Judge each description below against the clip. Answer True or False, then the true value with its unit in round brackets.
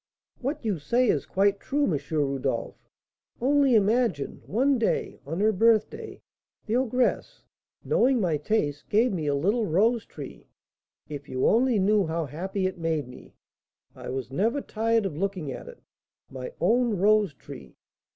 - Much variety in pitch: True (6.9 semitones)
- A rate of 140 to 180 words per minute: True (155 wpm)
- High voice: True (205 Hz)